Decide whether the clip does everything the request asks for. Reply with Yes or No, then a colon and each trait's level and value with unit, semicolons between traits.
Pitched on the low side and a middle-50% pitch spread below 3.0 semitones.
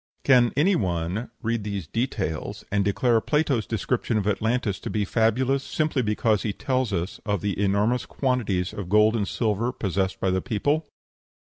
No: low, 110 Hz; average, 4.0 semitones